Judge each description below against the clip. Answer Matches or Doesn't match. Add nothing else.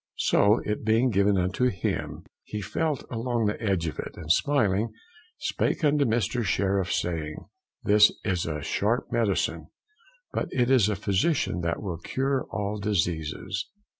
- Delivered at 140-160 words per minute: Matches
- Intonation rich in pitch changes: Doesn't match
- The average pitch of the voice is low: Matches